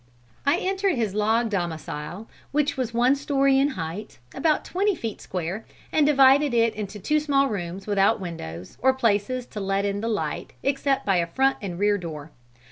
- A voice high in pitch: Yes, high, 220 Hz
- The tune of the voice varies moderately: No, wide, 6.0 semitones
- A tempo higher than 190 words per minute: No, average, 175 wpm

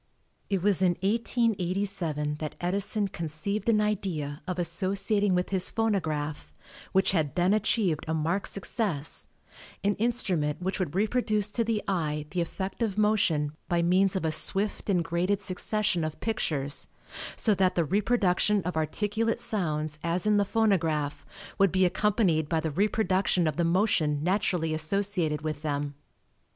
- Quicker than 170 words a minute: No, average, 150 wpm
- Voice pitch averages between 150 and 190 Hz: Yes, medium, 185 Hz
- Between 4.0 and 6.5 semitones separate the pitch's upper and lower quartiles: Yes, average, 4.5 semitones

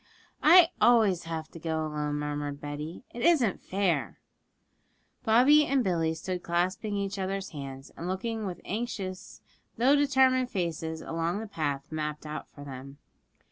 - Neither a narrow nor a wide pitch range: No, wide, 6.4 semitones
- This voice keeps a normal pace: Yes, average, 145 wpm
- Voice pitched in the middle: Yes, medium, 175 Hz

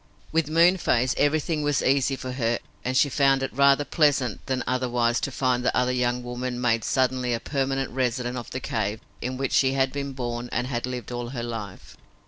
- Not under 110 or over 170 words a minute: No, average, 200 wpm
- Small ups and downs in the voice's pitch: Yes, narrow, 2.0 semitones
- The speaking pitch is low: Yes, low, 130 Hz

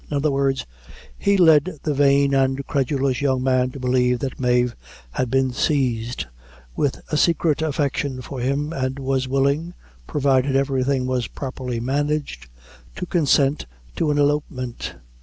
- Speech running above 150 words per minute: No, average, 145 wpm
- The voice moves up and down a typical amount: No, narrow, 2.1 semitones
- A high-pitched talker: No, low, 135 Hz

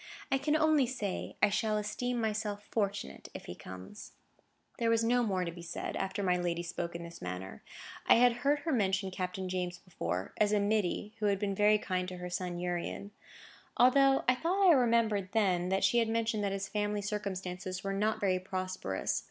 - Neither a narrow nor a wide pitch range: Yes, average, 3.7 semitones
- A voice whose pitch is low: No, high, 200 Hz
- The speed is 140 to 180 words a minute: No, average, 195 wpm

